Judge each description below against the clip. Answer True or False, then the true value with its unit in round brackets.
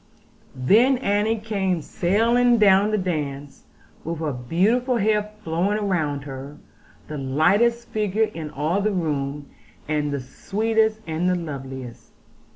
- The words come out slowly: True (130 wpm)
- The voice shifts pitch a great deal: True (6.5 semitones)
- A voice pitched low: False (180 Hz)